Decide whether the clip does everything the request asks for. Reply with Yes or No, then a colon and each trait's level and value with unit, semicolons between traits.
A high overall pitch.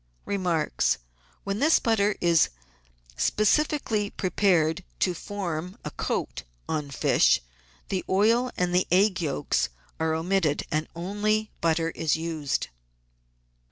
No: medium, 180 Hz